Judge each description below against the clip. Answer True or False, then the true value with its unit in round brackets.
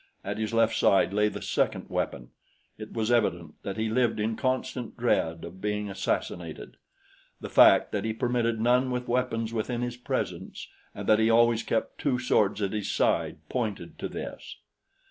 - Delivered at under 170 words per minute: False (175 wpm)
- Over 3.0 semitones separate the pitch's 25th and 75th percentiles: False (2.6 semitones)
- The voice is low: True (110 Hz)